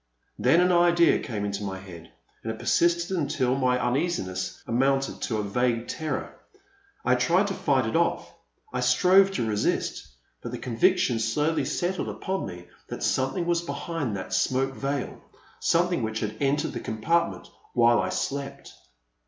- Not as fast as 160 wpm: No, average, 170 wpm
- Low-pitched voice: Yes, low, 130 Hz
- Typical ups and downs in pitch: No, wide, 7.3 semitones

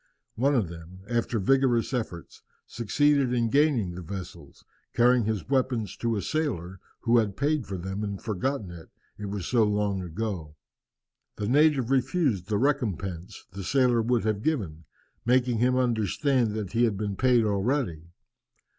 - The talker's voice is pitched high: No, low, 110 Hz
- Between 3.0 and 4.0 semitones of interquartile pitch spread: No, average, 4.8 semitones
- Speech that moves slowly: No, average, 155 wpm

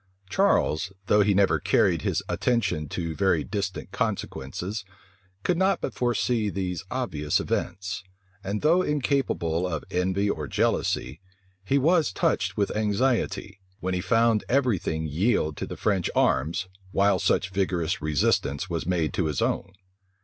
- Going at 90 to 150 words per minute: Yes, average, 145 wpm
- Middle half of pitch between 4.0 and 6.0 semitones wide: Yes, average, 5.1 semitones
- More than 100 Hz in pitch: No, very low, 95 Hz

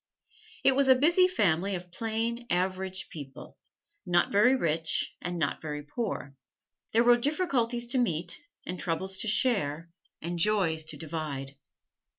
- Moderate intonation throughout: No, wide, 6.6 semitones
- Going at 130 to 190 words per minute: Yes, average, 145 wpm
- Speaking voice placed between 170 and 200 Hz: Yes, medium, 185 Hz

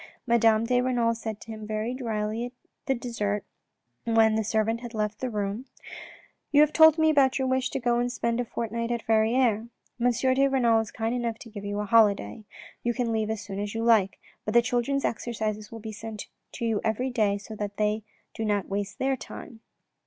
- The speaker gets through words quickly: Yes, fast, 210 wpm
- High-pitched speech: Yes, high, 225 Hz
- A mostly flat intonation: Yes, narrow, 2.3 semitones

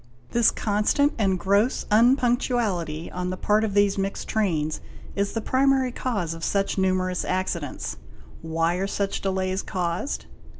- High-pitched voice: Yes, high, 195 Hz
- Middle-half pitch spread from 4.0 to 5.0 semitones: No, average, 3.4 semitones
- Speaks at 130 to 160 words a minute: Yes, average, 140 wpm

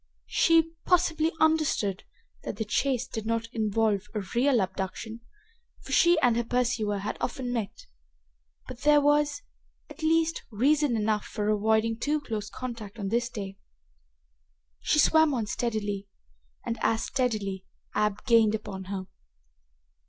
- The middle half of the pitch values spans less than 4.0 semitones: No, average, 5.2 semitones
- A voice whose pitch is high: Yes, high, 230 Hz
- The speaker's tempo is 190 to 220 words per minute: No, slow, 135 wpm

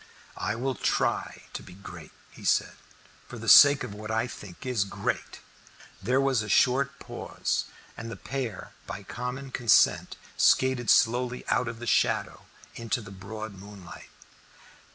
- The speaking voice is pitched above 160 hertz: No, low, 115 Hz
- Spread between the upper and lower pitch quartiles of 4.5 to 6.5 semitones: No, average, 3.7 semitones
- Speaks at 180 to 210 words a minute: No, average, 155 wpm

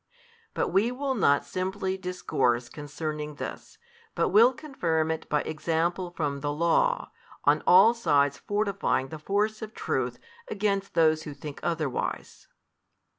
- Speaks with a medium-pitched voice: Yes, medium, 170 Hz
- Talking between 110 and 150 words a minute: Yes, average, 140 wpm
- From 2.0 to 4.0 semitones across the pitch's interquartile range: No, average, 5.3 semitones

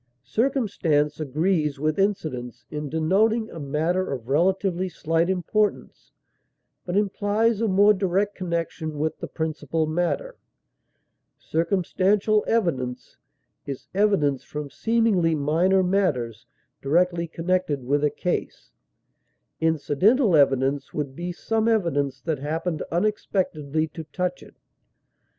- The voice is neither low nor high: Yes, medium, 170 Hz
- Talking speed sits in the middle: No, slow, 110 wpm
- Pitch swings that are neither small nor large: Yes, average, 4.7 semitones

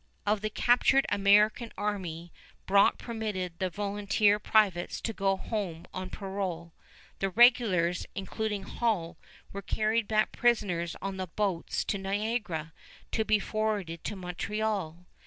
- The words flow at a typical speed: No, slow, 130 wpm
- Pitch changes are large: No, average, 3.0 semitones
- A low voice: No, high, 200 Hz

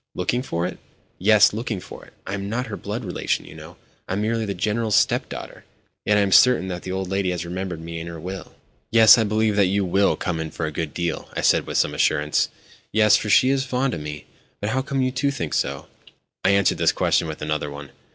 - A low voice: Yes, low, 100 Hz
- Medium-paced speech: No, fast, 240 wpm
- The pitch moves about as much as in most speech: Yes, average, 4.4 semitones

